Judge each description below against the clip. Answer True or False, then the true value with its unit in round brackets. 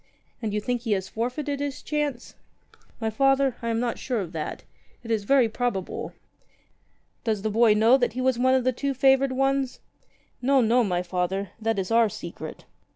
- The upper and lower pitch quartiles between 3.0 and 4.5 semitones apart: True (3.8 semitones)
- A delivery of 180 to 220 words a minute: True (195 wpm)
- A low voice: False (235 Hz)